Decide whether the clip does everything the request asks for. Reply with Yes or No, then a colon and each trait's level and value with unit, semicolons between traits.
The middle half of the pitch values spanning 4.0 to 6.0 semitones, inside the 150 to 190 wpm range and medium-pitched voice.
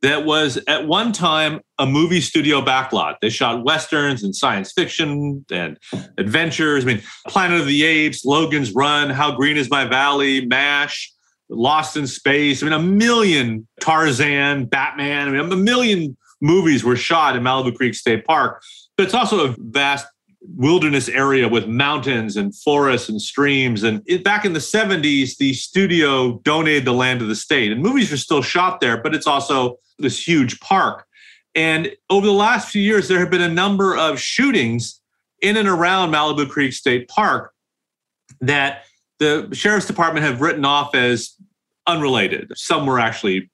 Yes: average, 4.6 semitones; average, 170 wpm; medium, 145 Hz